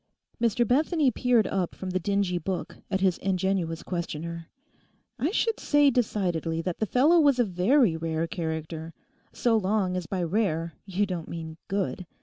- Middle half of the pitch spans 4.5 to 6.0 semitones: Yes, average, 5.2 semitones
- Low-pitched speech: No, high, 190 Hz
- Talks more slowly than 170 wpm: Yes, average, 160 wpm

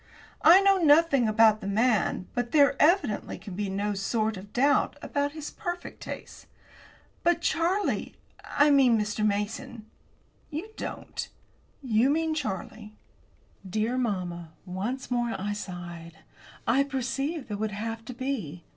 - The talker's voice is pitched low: No, high, 235 Hz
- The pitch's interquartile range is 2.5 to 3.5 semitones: No, wide, 5.6 semitones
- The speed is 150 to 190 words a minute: No, average, 140 wpm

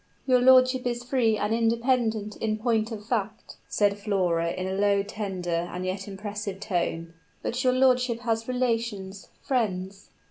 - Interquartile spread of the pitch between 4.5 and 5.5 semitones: No, average, 3.7 semitones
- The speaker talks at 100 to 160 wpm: Yes, average, 150 wpm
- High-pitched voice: Yes, high, 215 Hz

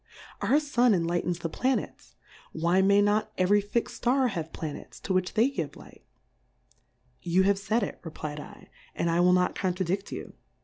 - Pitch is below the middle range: No, high, 190 Hz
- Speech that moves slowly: No, average, 175 wpm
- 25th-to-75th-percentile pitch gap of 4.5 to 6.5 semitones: No, average, 3.8 semitones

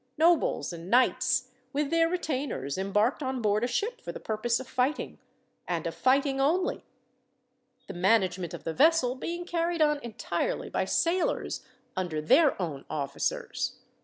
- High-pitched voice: Yes, very high, 255 Hz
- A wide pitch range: Yes, wide, 7.9 semitones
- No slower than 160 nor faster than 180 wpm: No, average, 150 wpm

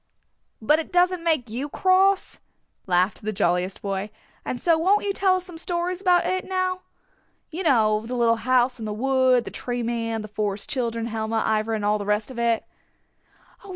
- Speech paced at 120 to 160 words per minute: No, average, 190 wpm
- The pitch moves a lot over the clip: Yes, wide, 8.1 semitones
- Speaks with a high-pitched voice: Yes, high, 240 Hz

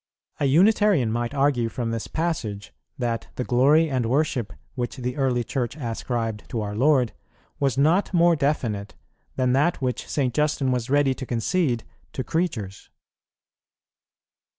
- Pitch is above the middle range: No, low, 130 Hz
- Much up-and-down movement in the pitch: No, average, 4.1 semitones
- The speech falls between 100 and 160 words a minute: Yes, average, 150 wpm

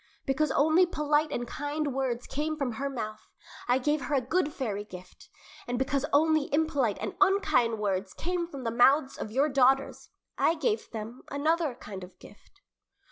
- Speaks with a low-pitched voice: No, very high, 270 Hz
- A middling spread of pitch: Yes, average, 4.5 semitones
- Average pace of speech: Yes, average, 175 wpm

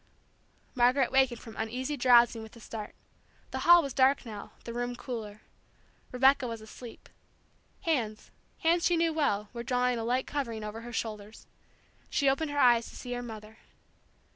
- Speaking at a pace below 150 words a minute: No, average, 165 wpm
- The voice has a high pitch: Yes, high, 245 Hz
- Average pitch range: Yes, average, 3.1 semitones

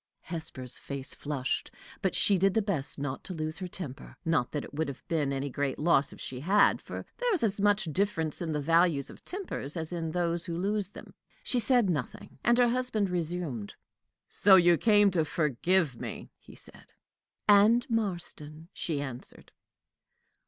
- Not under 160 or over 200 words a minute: Yes, average, 180 wpm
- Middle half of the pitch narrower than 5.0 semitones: No, wide, 5.5 semitones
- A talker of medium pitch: Yes, medium, 170 Hz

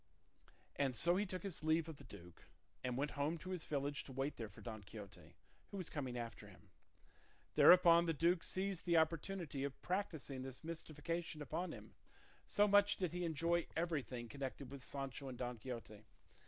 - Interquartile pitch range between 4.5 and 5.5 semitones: Yes, average, 4.8 semitones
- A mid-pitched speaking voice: Yes, medium, 150 Hz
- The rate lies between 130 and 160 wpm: No, average, 180 wpm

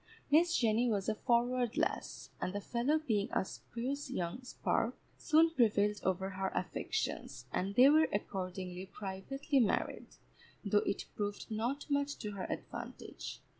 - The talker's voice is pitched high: Yes, high, 220 Hz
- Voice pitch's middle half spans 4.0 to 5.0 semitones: No, wide, 5.6 semitones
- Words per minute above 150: No, average, 145 wpm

